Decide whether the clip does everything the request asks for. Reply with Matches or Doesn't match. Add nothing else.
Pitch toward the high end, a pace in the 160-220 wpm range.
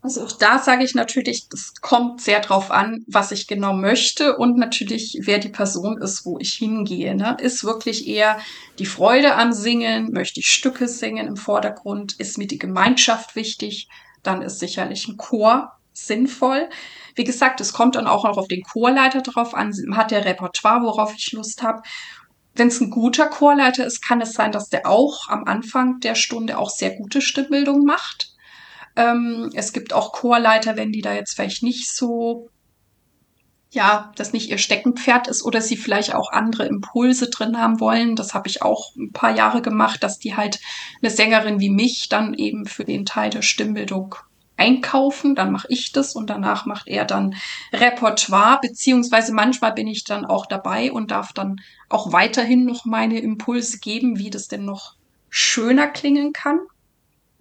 Matches